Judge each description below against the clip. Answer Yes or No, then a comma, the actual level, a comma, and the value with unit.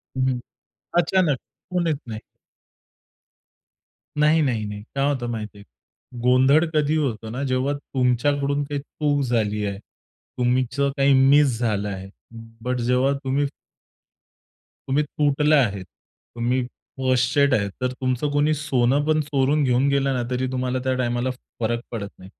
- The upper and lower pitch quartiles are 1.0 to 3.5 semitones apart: Yes, average, 2.9 semitones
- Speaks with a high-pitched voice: No, low, 130 Hz